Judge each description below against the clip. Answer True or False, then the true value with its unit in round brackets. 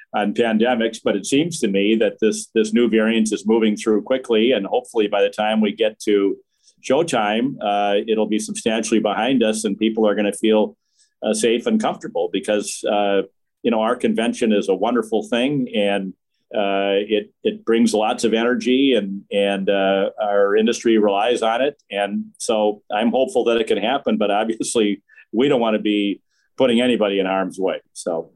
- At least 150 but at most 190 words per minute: True (185 wpm)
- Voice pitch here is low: True (105 Hz)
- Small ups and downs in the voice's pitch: True (2.1 semitones)